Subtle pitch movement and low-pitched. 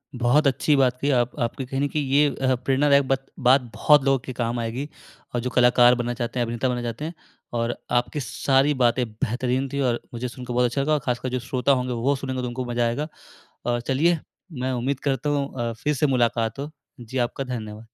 Yes: narrow, 2.2 semitones; low, 125 Hz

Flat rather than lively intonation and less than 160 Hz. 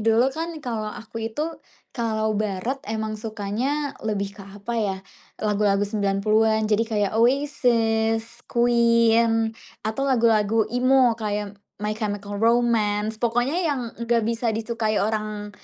No: narrow, 2.0 semitones; high, 220 Hz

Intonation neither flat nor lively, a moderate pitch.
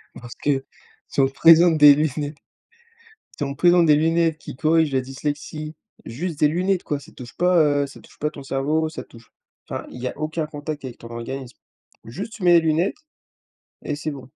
Yes: average, 3.1 semitones; medium, 150 Hz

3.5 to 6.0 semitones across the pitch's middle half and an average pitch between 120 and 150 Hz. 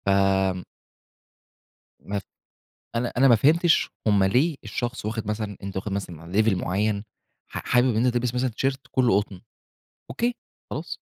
No: average, 4.1 semitones; low, 110 Hz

